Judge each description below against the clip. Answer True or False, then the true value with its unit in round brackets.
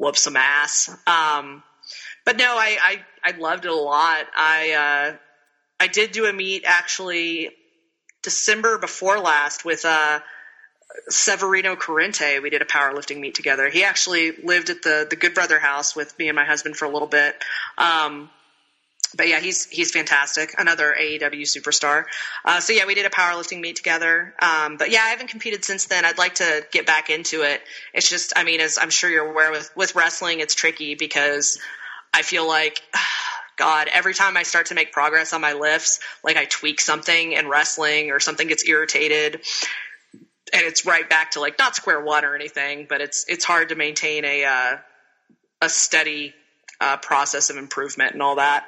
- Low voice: False (155 Hz)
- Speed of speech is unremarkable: True (185 wpm)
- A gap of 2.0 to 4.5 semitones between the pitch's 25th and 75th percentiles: True (3.0 semitones)